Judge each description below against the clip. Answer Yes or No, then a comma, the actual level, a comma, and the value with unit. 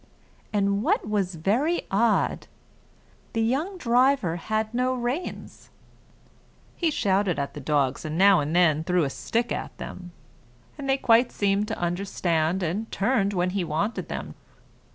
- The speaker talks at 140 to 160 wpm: Yes, average, 150 wpm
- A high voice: Yes, high, 200 Hz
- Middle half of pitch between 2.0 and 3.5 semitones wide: No, average, 5.3 semitones